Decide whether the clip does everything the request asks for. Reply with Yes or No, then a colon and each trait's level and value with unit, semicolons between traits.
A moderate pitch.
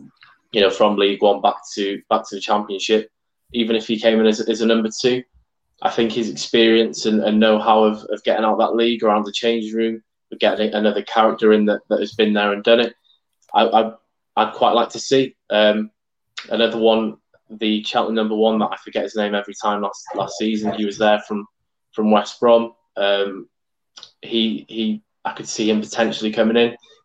No: low, 110 Hz